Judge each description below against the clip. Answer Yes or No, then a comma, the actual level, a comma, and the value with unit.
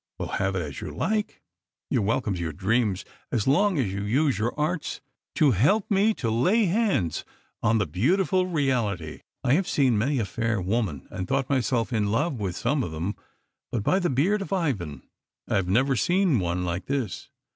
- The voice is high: No, low, 120 Hz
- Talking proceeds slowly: No, average, 200 wpm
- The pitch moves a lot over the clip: Yes, wide, 8.2 semitones